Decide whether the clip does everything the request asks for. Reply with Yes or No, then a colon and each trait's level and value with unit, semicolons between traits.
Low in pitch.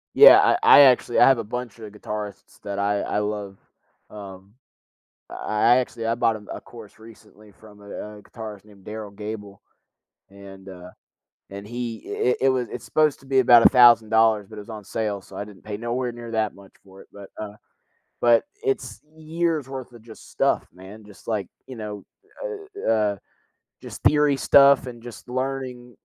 Yes: low, 110 Hz